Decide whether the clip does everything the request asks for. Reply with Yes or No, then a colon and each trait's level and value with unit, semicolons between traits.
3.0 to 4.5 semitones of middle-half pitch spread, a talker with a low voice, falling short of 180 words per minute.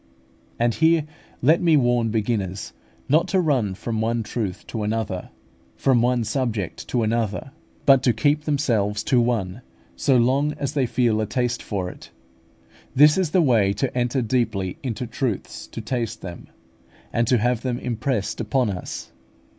Yes: average, 3.5 semitones; low, 120 Hz; average, 160 wpm